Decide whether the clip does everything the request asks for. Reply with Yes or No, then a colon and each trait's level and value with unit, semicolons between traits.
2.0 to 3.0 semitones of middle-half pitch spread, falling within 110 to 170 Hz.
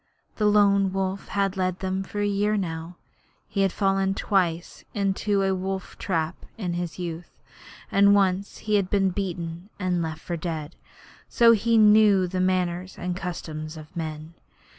No: narrow, 2.5 semitones; medium, 185 Hz